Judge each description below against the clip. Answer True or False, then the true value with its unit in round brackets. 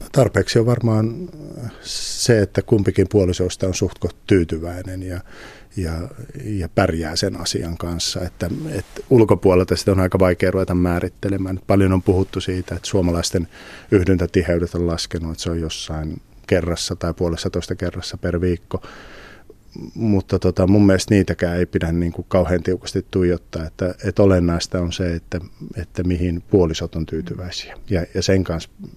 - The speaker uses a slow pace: False (145 wpm)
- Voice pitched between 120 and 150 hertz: False (90 Hz)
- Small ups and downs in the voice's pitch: True (2.1 semitones)